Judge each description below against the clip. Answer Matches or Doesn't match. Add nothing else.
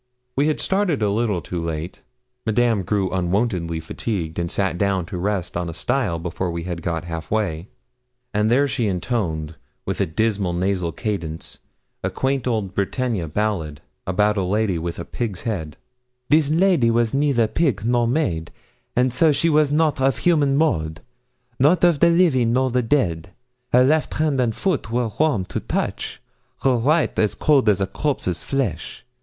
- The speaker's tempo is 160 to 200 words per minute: Matches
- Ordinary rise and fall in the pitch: Doesn't match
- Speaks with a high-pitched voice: Doesn't match